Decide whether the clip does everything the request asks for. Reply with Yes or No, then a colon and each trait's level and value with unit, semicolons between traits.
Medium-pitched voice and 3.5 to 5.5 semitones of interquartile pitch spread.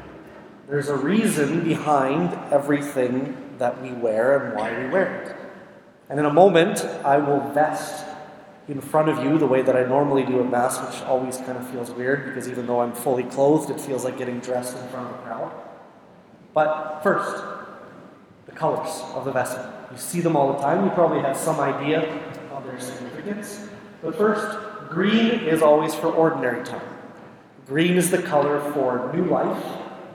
Yes: medium, 145 Hz; average, 3.9 semitones